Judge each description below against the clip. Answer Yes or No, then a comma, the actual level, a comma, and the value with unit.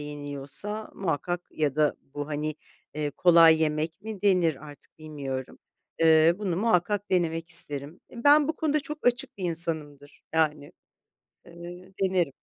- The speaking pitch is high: No, medium, 165 Hz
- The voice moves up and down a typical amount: Yes, average, 4.2 semitones